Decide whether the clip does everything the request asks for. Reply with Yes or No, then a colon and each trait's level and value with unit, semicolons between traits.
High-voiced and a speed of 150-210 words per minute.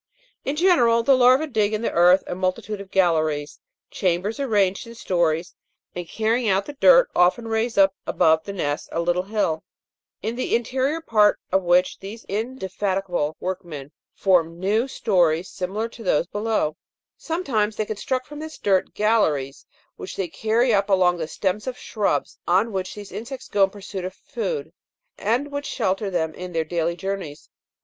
Yes: high, 195 Hz; average, 170 wpm